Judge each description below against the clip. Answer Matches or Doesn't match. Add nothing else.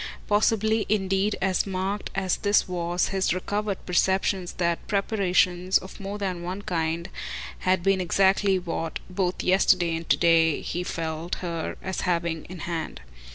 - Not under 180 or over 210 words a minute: Doesn't match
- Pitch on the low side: Doesn't match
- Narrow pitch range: Matches